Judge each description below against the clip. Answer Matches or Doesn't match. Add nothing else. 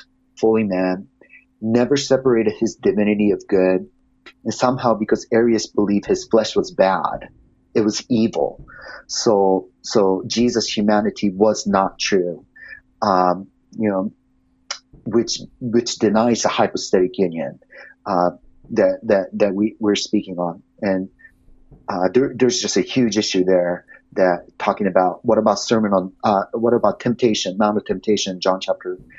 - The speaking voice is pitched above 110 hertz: Doesn't match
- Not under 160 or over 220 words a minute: Doesn't match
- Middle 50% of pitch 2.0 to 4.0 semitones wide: Matches